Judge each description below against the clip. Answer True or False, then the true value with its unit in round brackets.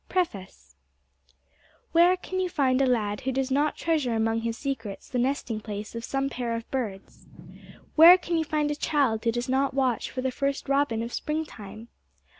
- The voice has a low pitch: False (260 Hz)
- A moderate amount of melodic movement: True (4.5 semitones)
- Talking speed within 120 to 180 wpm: False (190 wpm)